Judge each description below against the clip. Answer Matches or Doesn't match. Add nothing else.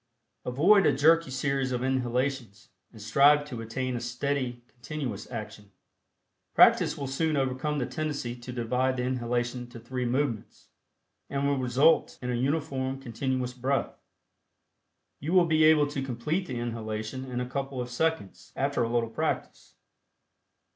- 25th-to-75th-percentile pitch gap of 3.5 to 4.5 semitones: Doesn't match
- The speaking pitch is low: Matches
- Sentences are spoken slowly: Doesn't match